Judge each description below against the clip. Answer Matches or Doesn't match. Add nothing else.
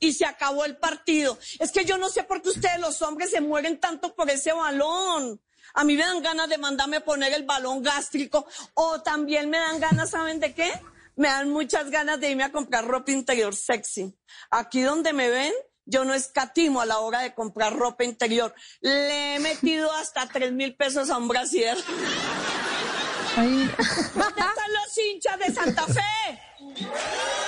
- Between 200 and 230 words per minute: Doesn't match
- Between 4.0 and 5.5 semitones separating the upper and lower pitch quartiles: Doesn't match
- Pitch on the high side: Matches